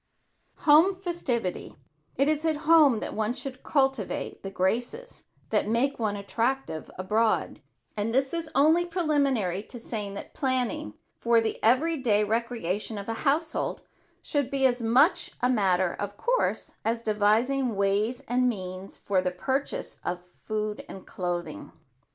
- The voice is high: Yes, high, 235 Hz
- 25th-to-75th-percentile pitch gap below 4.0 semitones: No, average, 5.2 semitones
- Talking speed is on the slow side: No, average, 150 wpm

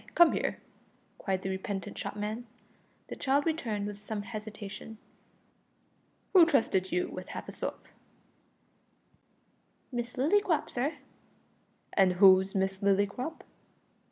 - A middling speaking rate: No, slow, 110 wpm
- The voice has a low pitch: No, high, 210 Hz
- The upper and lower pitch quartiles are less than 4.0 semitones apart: No, average, 4.8 semitones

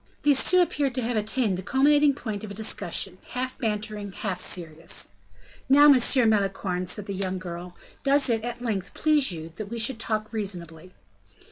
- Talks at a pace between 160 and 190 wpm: Yes, average, 175 wpm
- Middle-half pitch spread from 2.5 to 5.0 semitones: No, wide, 5.4 semitones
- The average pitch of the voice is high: Yes, high, 215 Hz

